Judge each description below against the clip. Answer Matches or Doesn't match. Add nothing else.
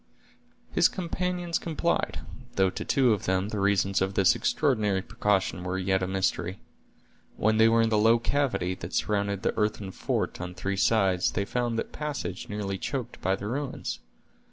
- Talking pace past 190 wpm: Doesn't match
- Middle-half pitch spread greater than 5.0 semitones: Doesn't match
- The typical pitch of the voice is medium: Doesn't match